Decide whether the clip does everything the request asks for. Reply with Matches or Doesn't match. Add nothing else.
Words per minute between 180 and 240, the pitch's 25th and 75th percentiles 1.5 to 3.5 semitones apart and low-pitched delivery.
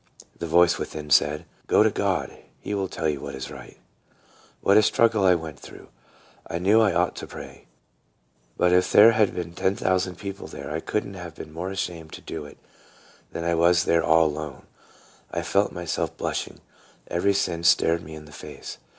Matches